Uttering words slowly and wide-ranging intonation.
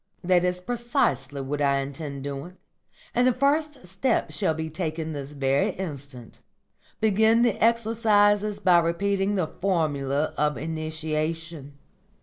Yes: slow, 130 wpm; wide, 6.2 semitones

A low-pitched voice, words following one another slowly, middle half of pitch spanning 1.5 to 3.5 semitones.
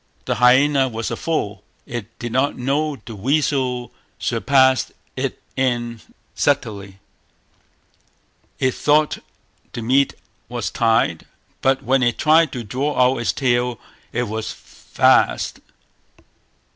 Yes: low, 125 Hz; slow, 120 wpm; average, 2.9 semitones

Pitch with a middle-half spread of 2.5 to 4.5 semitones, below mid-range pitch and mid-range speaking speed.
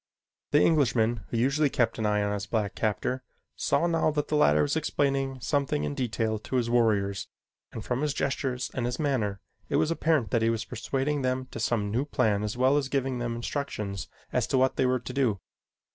No: average, 3.9 semitones; low, 125 Hz; fast, 210 wpm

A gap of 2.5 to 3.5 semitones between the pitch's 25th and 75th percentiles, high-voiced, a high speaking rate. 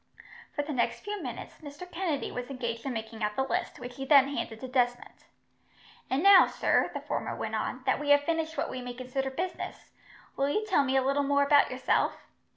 Yes: average, 3.0 semitones; very high, 275 Hz; fast, 215 wpm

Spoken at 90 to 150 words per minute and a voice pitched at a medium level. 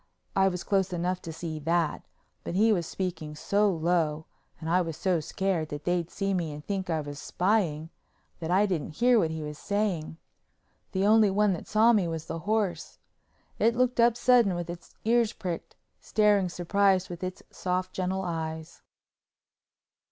No: average, 175 wpm; medium, 180 Hz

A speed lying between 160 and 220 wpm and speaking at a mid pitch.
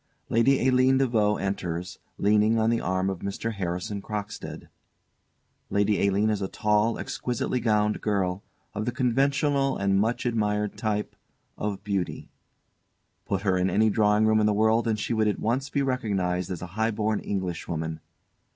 No: average, 165 wpm; low, 105 Hz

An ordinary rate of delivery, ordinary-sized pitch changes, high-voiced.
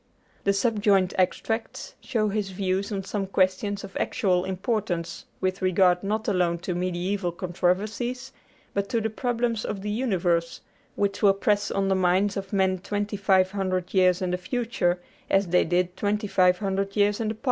No: average, 175 wpm; narrow, 2.2 semitones; high, 195 Hz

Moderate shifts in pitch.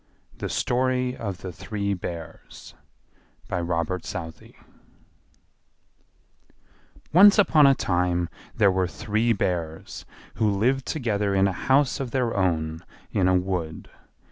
No: wide, 5.9 semitones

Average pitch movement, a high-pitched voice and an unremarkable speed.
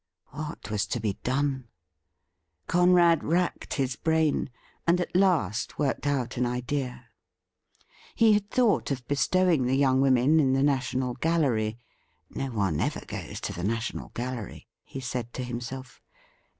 No: average, 4.4 semitones; low, 130 Hz; average, 155 wpm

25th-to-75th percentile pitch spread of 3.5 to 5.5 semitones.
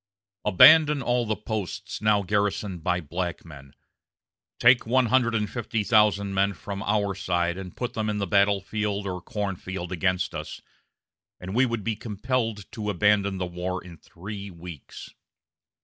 No: average, 2.9 semitones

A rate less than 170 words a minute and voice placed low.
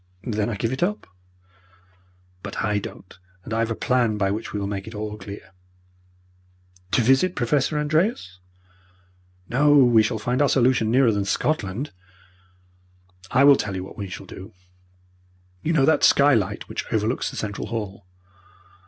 Yes: average, 160 wpm; low, 110 Hz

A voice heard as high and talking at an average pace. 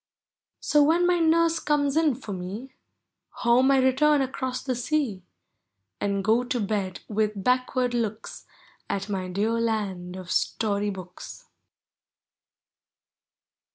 No: high, 235 Hz; slow, 120 wpm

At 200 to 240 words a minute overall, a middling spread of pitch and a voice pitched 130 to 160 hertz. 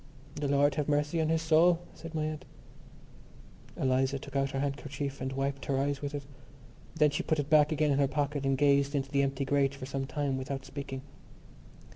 No: fast, 205 wpm; narrow, 1.5 semitones; medium, 140 Hz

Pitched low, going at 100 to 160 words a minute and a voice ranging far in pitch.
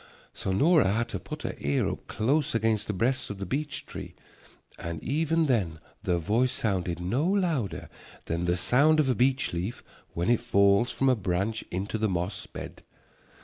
No: low, 110 Hz; average, 185 wpm; wide, 6.4 semitones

